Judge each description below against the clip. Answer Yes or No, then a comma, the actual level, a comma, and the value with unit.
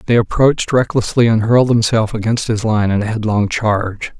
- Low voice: Yes, low, 110 Hz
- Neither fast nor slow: Yes, average, 185 wpm